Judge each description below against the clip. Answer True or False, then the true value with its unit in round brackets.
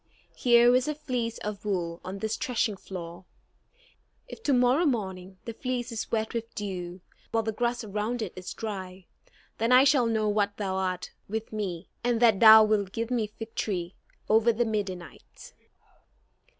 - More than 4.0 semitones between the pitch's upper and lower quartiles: False (3.7 semitones)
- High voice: True (220 Hz)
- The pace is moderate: True (165 wpm)